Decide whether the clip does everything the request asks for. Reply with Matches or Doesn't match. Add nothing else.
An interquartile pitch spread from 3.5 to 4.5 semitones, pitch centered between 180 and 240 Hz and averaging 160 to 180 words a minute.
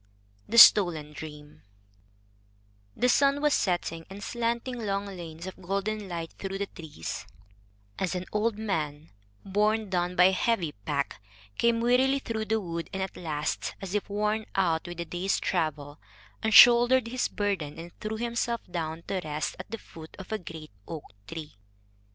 Doesn't match